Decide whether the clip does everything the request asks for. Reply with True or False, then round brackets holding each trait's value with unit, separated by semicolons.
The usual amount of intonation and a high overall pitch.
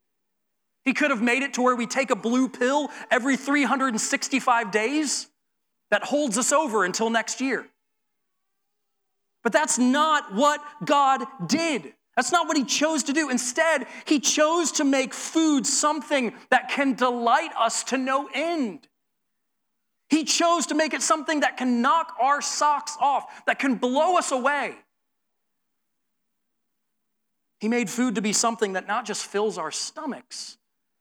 True (4.0 semitones; 265 Hz)